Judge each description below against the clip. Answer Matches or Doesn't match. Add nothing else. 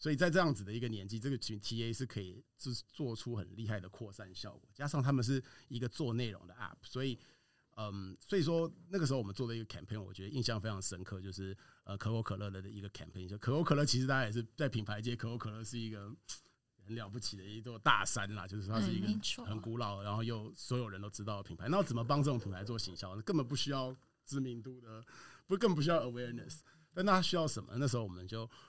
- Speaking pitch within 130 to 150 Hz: Doesn't match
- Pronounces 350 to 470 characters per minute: Matches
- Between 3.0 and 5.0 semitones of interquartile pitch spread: Matches